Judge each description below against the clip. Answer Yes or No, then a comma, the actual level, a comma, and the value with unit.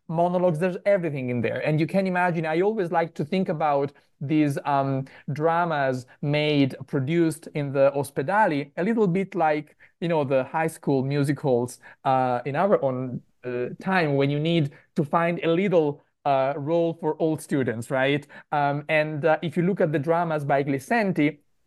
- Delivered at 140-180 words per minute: Yes, average, 175 wpm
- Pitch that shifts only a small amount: No, average, 3.4 semitones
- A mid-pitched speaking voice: Yes, medium, 155 Hz